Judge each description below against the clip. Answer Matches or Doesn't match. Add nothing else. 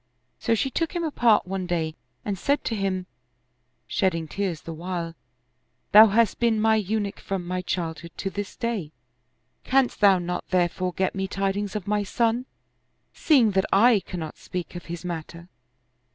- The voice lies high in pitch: Matches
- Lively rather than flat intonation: Doesn't match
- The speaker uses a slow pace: Doesn't match